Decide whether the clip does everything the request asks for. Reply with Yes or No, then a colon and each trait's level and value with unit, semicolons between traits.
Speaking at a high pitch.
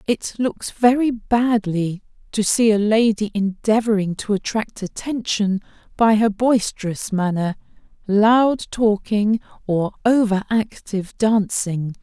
Yes: high, 210 Hz